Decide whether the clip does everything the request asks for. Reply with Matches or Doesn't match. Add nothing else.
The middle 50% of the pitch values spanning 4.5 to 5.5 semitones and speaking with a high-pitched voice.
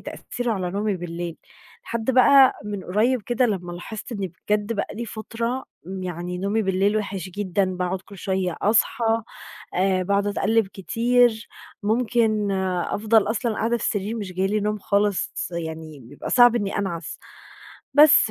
Doesn't match